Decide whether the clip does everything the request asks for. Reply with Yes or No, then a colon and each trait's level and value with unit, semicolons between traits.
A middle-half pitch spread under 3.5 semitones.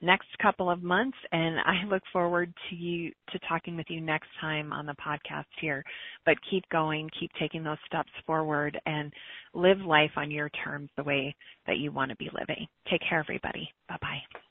Yes: average, 2.7 semitones